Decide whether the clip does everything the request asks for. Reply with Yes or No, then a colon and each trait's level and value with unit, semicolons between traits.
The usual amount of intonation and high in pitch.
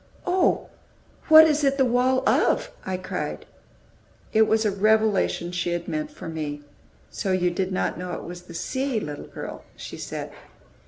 No: wide, 7.0 semitones; high, 205 Hz